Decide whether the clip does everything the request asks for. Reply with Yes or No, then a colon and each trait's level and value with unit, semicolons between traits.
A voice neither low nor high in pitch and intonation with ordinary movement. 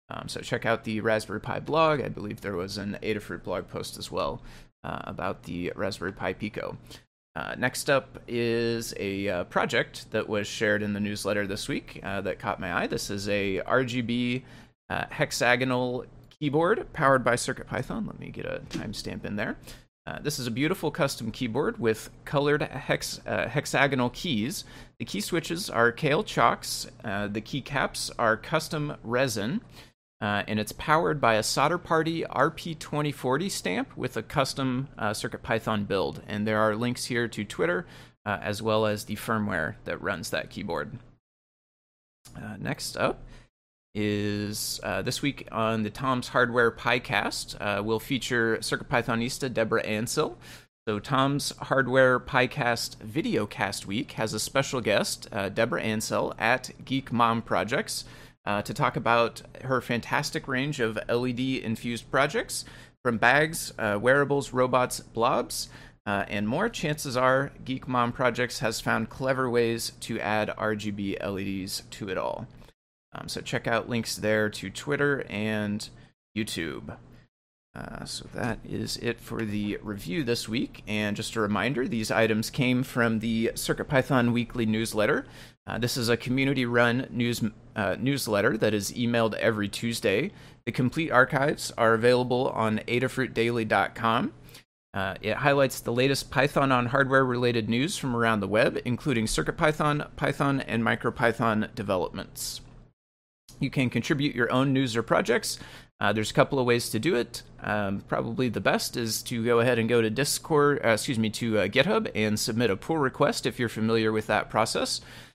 No: low, 120 Hz; average, 3.4 semitones